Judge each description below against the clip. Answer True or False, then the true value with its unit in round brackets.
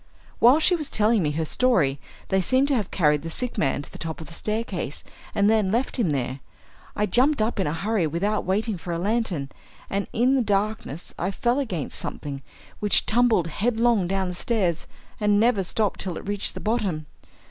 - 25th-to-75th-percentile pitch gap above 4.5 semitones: True (5.3 semitones)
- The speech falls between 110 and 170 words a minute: False (200 wpm)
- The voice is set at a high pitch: True (200 Hz)